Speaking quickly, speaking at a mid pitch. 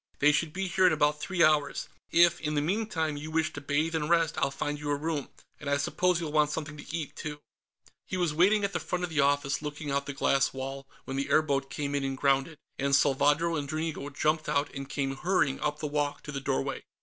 Yes: fast, 240 wpm; medium, 150 Hz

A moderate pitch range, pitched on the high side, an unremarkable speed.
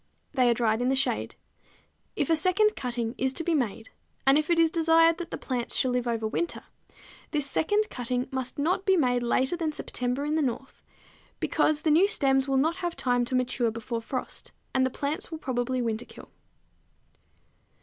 Yes: average, 4.7 semitones; very high, 265 Hz; average, 190 wpm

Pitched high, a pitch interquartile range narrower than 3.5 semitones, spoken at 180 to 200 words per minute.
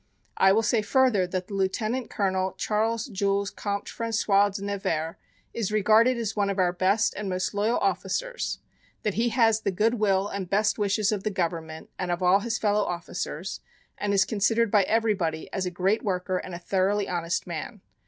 Yes: high, 200 Hz; narrow, 2.6 semitones; average, 190 wpm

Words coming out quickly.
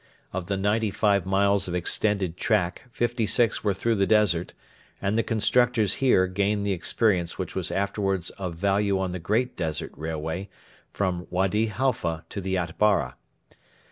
No: average, 160 wpm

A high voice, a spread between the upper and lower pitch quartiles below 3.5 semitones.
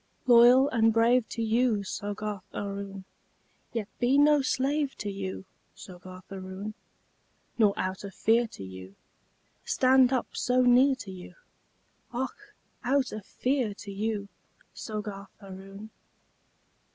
No: high, 215 Hz; average, 4.3 semitones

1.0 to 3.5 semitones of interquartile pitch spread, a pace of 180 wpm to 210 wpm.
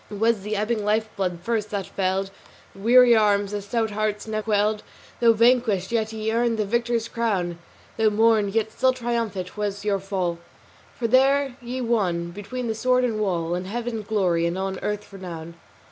Yes: average, 3.0 semitones; average, 185 wpm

